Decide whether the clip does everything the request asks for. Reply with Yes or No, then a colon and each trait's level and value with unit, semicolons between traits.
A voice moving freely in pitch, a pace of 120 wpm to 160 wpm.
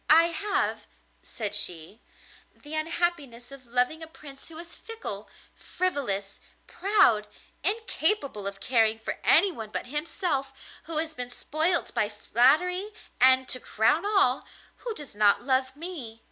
Yes: wide, 6.5 semitones; slow, 135 wpm